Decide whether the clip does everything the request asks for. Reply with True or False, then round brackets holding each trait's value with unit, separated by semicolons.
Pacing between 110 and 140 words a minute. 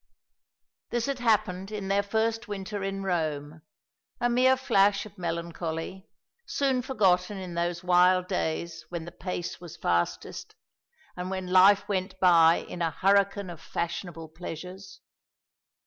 True (135 wpm)